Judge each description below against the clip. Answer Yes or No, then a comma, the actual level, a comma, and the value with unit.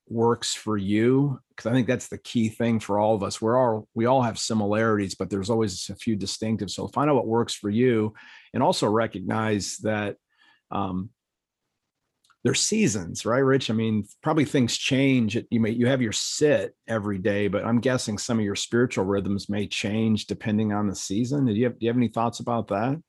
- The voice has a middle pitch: No, low, 110 Hz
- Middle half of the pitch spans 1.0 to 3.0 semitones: Yes, average, 2.7 semitones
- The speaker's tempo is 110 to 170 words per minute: No, fast, 205 wpm